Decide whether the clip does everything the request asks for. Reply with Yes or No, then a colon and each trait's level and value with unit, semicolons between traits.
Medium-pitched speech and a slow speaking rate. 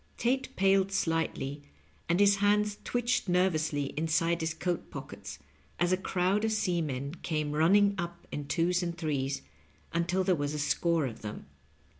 No: medium, 170 Hz; average, 160 wpm